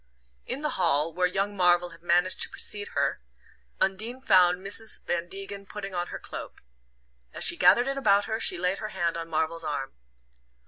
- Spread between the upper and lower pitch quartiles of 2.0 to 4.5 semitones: Yes, average, 2.8 semitones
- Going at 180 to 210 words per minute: Yes, average, 185 wpm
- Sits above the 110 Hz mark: Yes, medium, 185 Hz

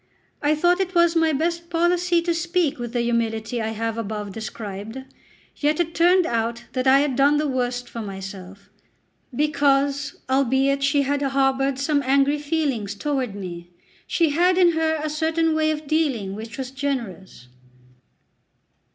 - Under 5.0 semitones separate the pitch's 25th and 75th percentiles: No, wide, 5.4 semitones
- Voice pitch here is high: Yes, very high, 275 Hz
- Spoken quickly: No, average, 160 wpm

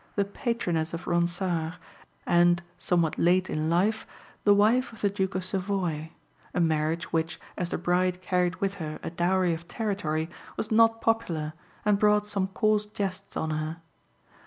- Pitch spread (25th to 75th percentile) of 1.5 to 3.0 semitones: No, average, 3.5 semitones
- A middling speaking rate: Yes, average, 160 wpm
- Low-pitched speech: No, medium, 180 Hz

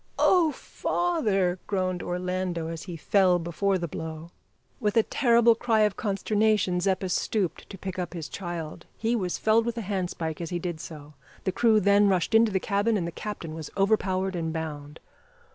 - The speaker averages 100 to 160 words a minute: No, average, 180 wpm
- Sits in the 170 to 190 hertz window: Yes, medium, 185 Hz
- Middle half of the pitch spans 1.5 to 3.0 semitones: No, average, 3.8 semitones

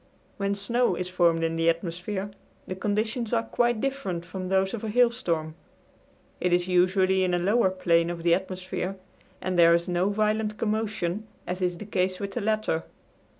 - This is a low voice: No, high, 190 Hz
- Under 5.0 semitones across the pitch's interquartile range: Yes, average, 3.3 semitones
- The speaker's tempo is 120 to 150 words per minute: No, average, 180 wpm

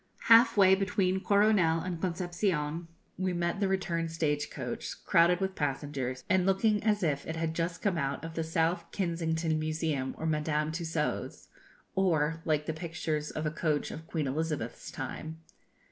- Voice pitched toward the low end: No, medium, 165 Hz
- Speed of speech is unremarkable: Yes, average, 160 wpm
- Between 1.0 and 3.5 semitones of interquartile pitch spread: Yes, average, 3.0 semitones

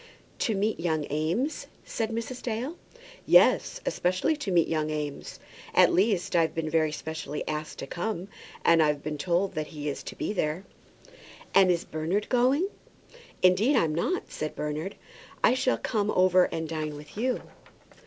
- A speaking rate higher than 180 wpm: No, average, 165 wpm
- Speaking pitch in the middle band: Yes, medium, 175 Hz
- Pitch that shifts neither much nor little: No, wide, 5.8 semitones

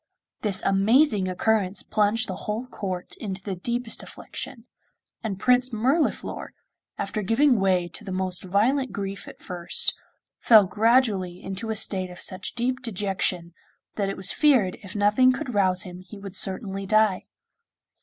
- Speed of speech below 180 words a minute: Yes, average, 155 wpm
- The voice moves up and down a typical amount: Yes, average, 3.5 semitones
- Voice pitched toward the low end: No, high, 205 Hz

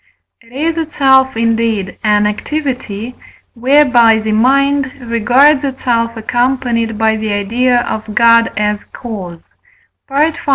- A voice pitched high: Yes, high, 235 Hz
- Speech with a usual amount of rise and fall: Yes, average, 3.3 semitones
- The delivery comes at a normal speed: No, slow, 115 wpm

